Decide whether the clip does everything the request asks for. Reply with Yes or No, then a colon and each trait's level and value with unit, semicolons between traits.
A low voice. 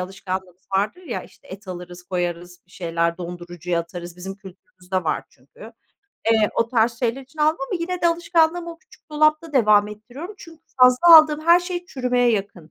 No: high, 215 Hz